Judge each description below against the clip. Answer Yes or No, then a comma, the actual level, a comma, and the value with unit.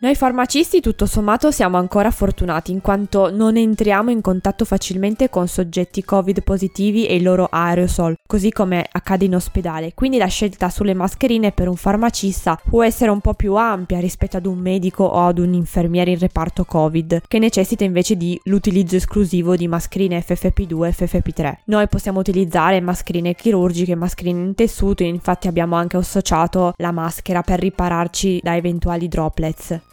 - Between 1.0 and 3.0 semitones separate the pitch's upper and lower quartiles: Yes, narrow, 2.5 semitones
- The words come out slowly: No, average, 165 wpm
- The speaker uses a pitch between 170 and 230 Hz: Yes, medium, 185 Hz